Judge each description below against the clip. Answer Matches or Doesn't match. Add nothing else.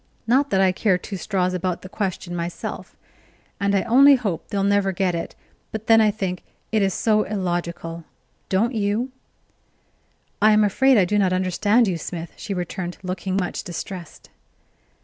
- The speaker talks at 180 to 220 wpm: Doesn't match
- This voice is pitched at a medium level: Doesn't match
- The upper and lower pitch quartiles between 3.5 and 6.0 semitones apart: Doesn't match